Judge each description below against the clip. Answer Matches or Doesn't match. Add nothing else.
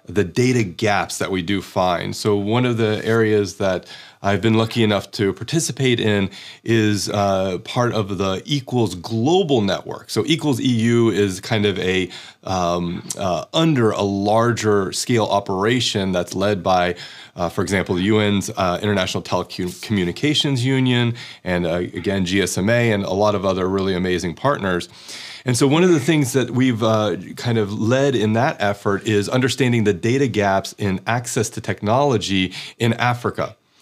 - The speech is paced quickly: Doesn't match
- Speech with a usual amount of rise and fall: Matches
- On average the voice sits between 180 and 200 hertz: Doesn't match